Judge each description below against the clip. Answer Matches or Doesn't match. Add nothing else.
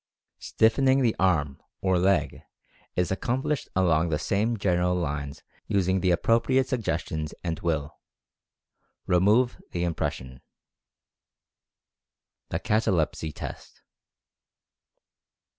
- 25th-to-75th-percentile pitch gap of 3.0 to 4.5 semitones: Doesn't match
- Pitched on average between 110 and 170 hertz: Doesn't match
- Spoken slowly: Matches